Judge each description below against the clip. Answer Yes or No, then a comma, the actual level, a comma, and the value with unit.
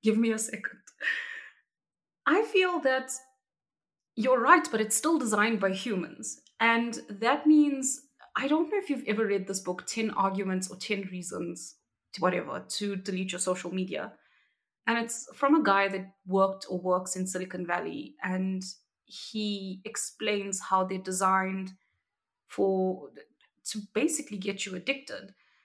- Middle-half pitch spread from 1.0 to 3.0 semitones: No, wide, 5.5 semitones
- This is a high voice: Yes, high, 205 Hz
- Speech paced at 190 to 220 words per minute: No, average, 145 wpm